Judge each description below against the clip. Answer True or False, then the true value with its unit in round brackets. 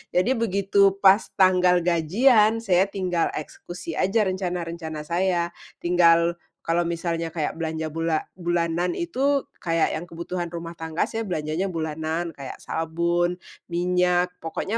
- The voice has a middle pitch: True (175 Hz)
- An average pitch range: False (2.1 semitones)